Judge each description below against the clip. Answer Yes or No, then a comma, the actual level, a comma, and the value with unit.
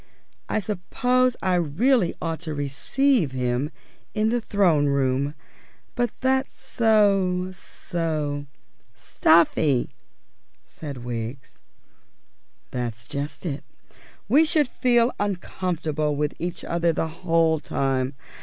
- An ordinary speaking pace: No, slow, 105 wpm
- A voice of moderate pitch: Yes, medium, 165 Hz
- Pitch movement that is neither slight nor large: No, wide, 6.7 semitones